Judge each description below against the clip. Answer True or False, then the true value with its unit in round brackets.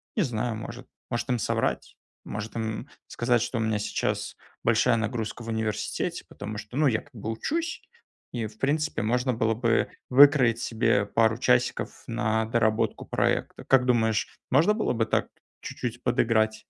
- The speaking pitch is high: False (115 Hz)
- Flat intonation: True (2.1 semitones)